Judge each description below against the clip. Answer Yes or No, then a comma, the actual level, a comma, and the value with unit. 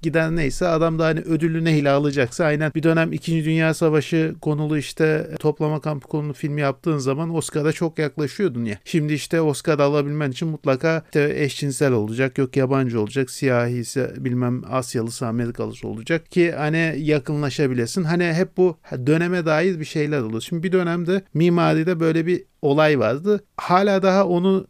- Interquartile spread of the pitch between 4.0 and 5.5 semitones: No, average, 3.2 semitones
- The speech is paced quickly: Yes, fast, 160 wpm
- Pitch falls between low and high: Yes, medium, 155 Hz